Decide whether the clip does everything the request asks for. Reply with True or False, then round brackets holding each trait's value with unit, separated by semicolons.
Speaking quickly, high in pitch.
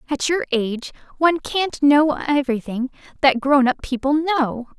False (150 wpm; 280 Hz)